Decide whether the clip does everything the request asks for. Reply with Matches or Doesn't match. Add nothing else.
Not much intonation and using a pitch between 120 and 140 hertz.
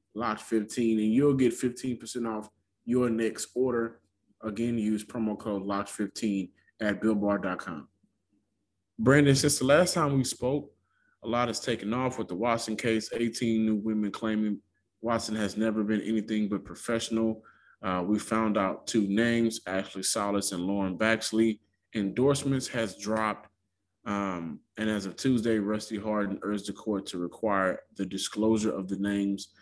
Doesn't match